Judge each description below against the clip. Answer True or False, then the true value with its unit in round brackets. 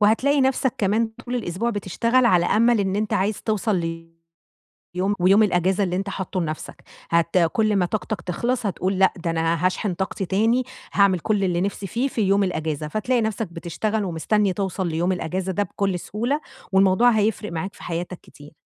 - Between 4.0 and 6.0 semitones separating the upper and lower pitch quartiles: False (3.4 semitones)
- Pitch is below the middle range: False (195 Hz)